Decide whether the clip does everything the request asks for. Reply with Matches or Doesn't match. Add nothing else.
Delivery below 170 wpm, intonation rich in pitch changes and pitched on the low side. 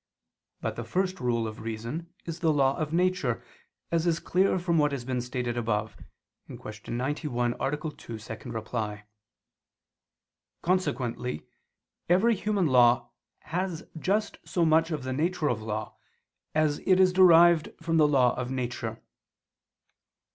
Doesn't match